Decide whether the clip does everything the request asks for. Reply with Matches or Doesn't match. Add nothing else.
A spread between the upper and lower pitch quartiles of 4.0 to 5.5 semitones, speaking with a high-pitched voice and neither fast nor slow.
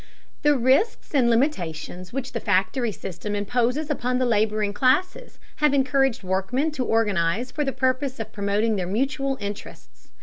Matches